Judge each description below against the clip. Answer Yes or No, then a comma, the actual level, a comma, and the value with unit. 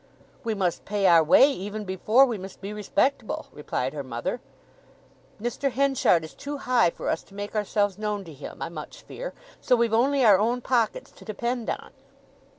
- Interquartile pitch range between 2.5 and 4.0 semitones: No, average, 4.5 semitones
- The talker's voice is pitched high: Yes, high, 215 Hz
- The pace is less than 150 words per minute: No, average, 185 wpm